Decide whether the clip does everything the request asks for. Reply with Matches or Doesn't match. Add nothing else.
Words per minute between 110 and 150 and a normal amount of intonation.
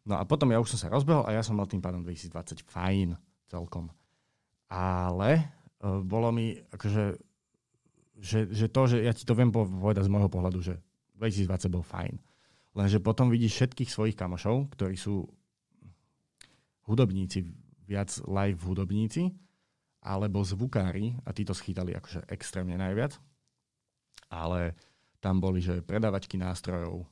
Matches